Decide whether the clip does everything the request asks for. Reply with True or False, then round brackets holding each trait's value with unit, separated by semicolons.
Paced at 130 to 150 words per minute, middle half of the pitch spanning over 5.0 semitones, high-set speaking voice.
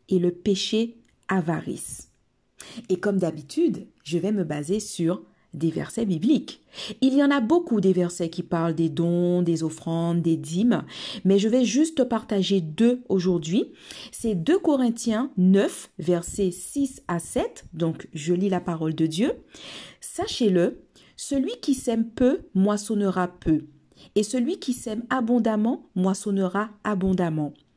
True (145 wpm; 5.4 semitones; 195 Hz)